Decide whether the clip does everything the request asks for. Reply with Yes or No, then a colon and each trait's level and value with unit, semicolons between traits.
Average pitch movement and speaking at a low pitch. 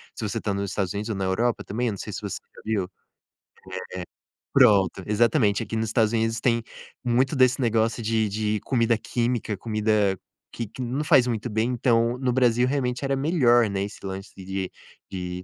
Yes: average, 3.1 semitones; low, 115 Hz